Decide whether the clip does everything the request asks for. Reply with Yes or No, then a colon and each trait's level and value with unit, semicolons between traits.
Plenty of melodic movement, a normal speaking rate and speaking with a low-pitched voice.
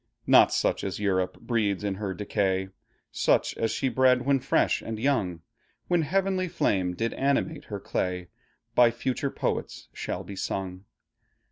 Yes: wide, 6.0 semitones; average, 150 wpm; low, 110 Hz